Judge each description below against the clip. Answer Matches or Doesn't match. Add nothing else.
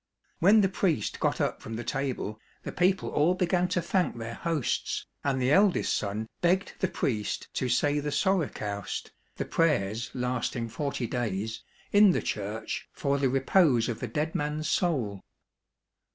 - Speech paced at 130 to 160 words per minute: Matches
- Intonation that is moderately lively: Doesn't match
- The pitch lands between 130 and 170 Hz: Matches